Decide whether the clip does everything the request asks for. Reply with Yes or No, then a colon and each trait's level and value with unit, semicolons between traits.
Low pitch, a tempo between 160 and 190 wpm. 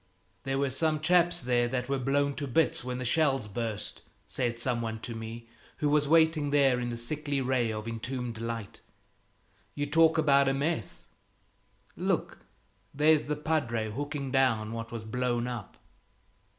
Yes: low, 130 Hz; average, 165 wpm